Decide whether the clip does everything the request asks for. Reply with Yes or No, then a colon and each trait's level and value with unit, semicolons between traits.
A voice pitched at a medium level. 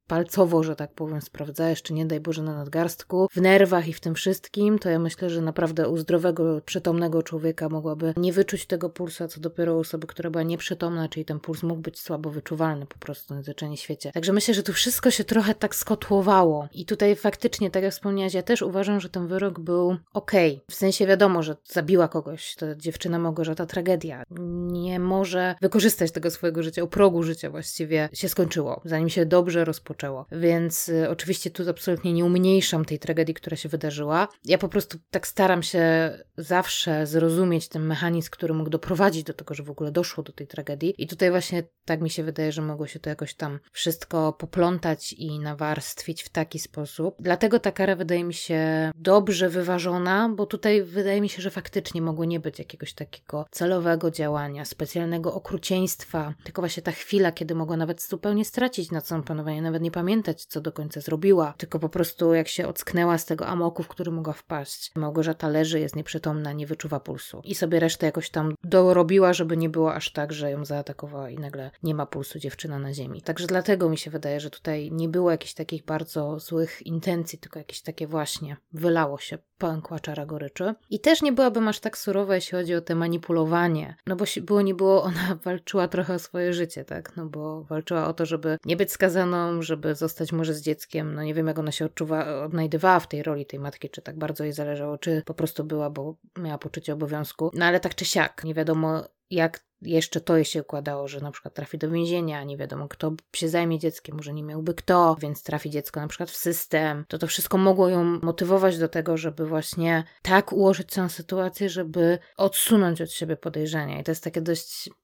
Yes: medium, 165 Hz